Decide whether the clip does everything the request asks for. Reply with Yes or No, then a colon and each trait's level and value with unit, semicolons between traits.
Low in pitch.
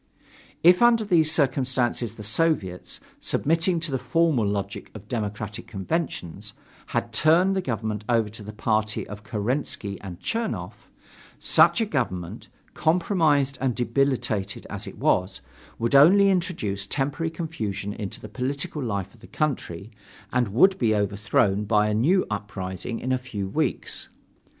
Yes: low, 120 Hz